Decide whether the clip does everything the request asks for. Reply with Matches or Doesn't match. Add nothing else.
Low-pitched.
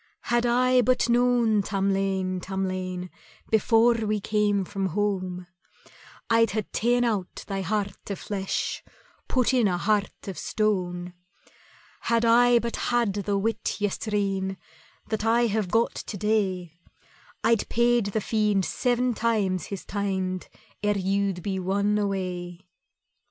Doesn't match